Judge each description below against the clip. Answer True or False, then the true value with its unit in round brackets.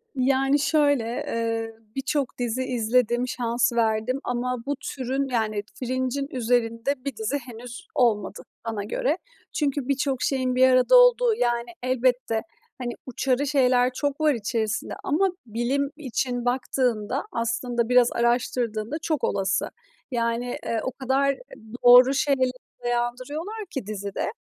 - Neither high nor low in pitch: False (250 Hz)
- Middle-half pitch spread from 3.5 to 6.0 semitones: False (2.7 semitones)